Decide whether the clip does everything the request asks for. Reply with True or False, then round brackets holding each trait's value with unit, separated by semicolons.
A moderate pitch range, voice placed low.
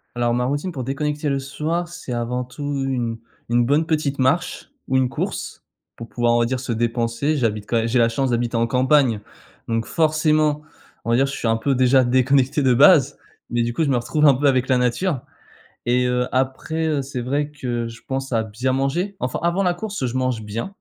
True (3.5 semitones; 130 Hz)